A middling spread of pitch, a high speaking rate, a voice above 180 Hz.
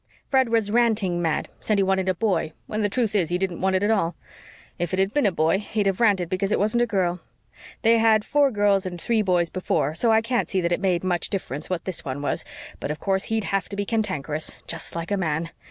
Yes: average, 3.8 semitones; fast, 250 wpm; high, 190 Hz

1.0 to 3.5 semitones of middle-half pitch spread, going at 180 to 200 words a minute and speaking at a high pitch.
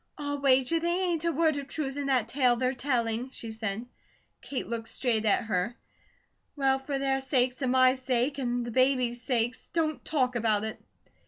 Yes: average, 2.8 semitones; average, 185 wpm; very high, 255 Hz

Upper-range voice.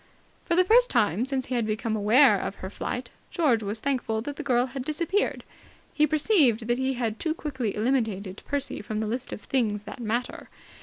Yes: high, 245 Hz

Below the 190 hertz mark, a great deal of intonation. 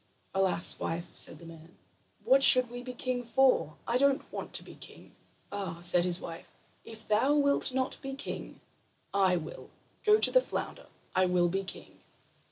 No: high, 215 Hz; wide, 6.9 semitones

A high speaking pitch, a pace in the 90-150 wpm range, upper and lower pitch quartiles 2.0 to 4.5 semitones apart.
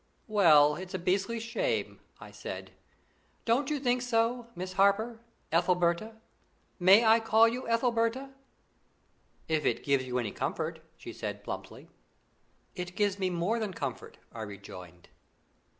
No: high, 200 Hz; slow, 135 wpm; average, 5.3 semitones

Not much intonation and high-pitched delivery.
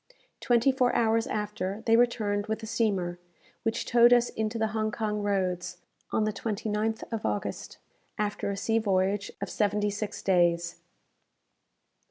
Yes: narrow, 2.1 semitones; high, 215 Hz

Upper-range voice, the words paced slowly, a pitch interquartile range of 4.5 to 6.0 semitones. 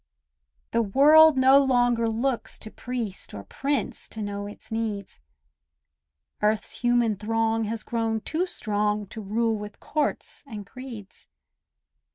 No: high, 225 Hz; slow, 130 wpm; average, 3.2 semitones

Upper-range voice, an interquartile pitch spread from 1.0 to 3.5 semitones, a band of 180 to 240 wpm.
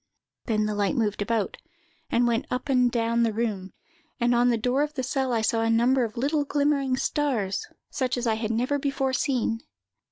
Yes: high, 240 Hz; average, 2.9 semitones; average, 200 wpm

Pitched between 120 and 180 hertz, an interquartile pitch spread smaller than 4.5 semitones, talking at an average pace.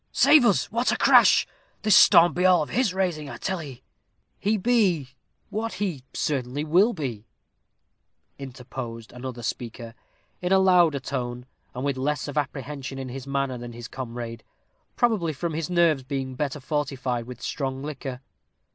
No: medium, 140 Hz; wide, 5.4 semitones; average, 160 wpm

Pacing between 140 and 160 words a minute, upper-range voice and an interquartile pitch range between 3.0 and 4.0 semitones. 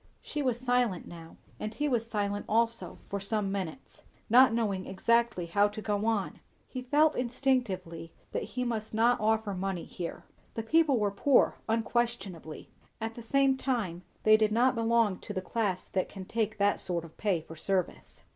No: average, 175 wpm; high, 220 Hz; average, 3.6 semitones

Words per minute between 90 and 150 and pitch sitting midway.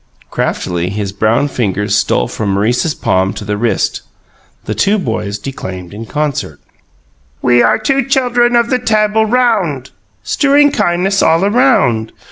Yes: average, 145 wpm; medium, 145 Hz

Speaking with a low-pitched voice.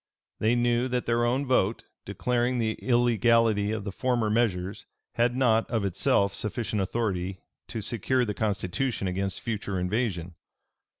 Yes: low, 110 Hz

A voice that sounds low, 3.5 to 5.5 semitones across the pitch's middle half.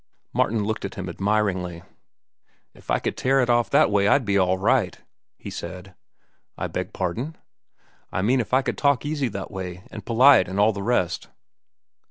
Yes: low, 105 Hz; average, 4.7 semitones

